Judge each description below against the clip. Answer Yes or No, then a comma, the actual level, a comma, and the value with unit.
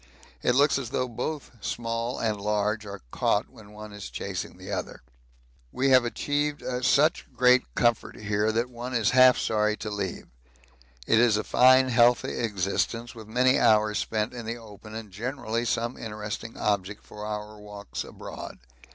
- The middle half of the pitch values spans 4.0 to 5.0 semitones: No, average, 2.8 semitones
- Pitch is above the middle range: No, low, 115 Hz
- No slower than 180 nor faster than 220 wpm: No, average, 165 wpm